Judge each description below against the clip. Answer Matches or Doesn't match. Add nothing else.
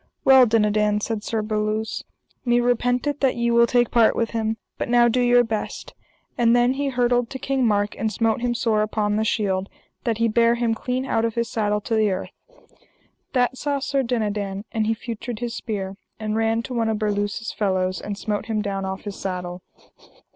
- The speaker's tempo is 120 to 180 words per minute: Doesn't match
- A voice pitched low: Doesn't match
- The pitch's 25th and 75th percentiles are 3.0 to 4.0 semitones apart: Doesn't match